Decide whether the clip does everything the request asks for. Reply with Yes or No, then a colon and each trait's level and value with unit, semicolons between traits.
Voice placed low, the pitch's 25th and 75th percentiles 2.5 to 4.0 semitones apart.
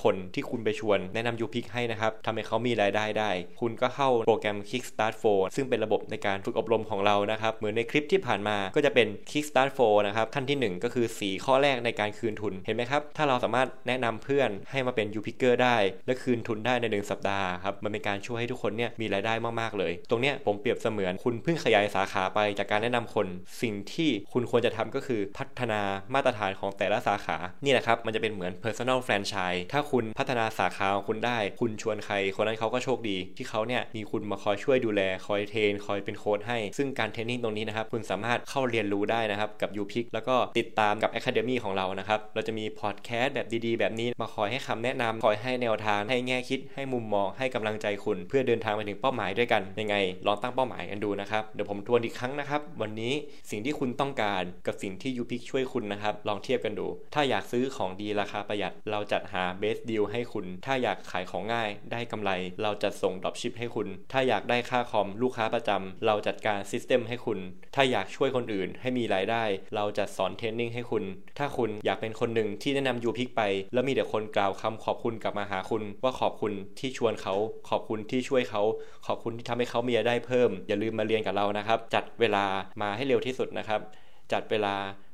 Yes: low, 110 Hz; average, 3.1 semitones